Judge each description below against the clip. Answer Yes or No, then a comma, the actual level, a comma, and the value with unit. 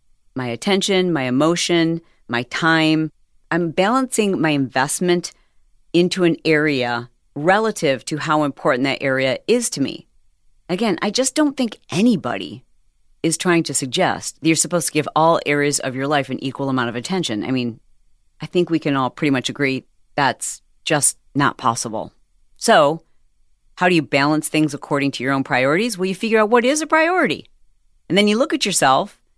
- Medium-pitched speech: Yes, medium, 155 Hz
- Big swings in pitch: Yes, wide, 5.8 semitones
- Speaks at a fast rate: No, average, 175 wpm